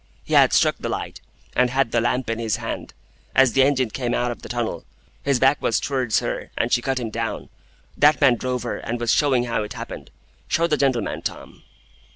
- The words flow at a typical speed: No, fast, 215 wpm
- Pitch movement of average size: No, narrow, 2.3 semitones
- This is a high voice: No, low, 125 Hz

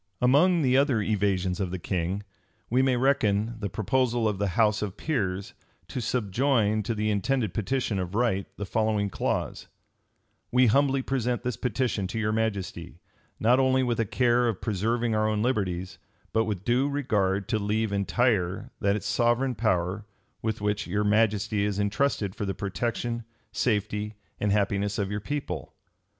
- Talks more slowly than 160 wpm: No, average, 165 wpm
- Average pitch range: Yes, average, 3.4 semitones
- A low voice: Yes, low, 110 Hz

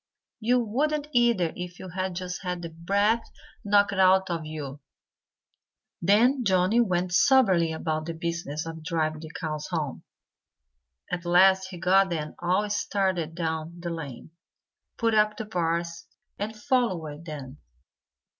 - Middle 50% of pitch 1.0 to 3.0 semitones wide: No, average, 3.9 semitones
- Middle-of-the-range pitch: Yes, medium, 180 Hz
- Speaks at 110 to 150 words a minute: Yes, average, 140 wpm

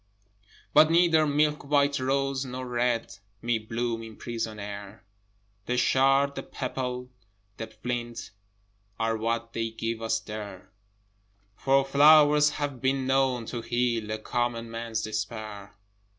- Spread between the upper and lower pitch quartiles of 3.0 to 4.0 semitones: Yes, average, 3.3 semitones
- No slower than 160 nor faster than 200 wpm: No, slow, 135 wpm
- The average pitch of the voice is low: Yes, low, 120 Hz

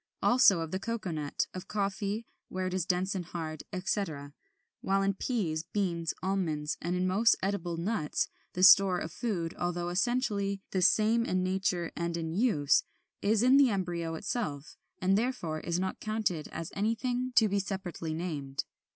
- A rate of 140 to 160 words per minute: No, average, 170 wpm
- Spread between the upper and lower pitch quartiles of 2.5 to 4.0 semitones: Yes, average, 3.5 semitones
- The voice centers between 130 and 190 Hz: Yes, medium, 185 Hz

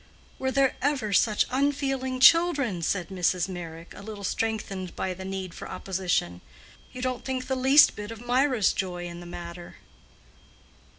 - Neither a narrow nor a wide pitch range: No, wide, 6.3 semitones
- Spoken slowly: No, average, 160 wpm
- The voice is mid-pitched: No, high, 210 Hz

